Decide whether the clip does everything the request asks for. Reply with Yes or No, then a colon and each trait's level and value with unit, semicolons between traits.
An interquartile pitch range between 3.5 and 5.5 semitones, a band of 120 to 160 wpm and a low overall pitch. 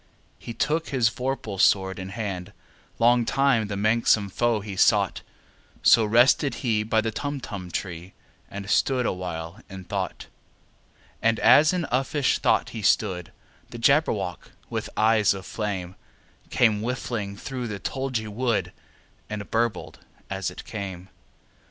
Yes: average, 3.9 semitones; average, 140 wpm; low, 110 Hz